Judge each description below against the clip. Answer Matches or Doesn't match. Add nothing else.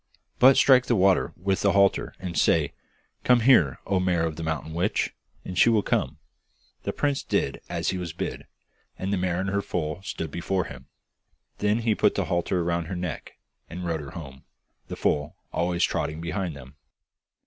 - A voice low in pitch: Matches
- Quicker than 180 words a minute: Matches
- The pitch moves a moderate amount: Matches